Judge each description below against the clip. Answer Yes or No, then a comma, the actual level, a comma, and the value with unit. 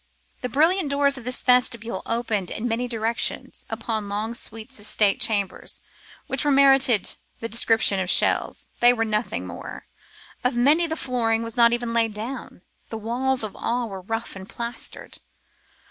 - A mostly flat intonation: Yes, narrow, 2.3 semitones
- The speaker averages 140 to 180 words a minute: Yes, average, 165 wpm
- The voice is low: No, high, 235 Hz